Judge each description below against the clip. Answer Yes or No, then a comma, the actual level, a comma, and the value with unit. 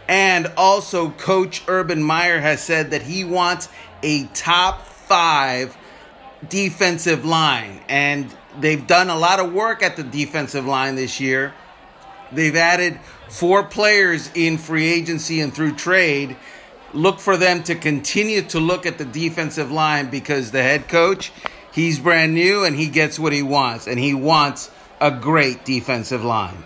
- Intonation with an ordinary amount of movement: Yes, average, 3.7 semitones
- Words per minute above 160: No, average, 155 wpm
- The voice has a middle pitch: Yes, medium, 160 Hz